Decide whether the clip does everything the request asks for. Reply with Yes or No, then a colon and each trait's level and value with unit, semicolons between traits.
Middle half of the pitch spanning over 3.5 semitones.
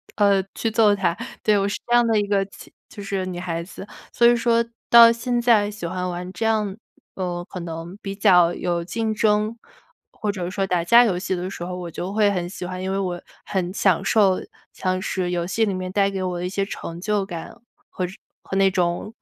No: average, 2.7 semitones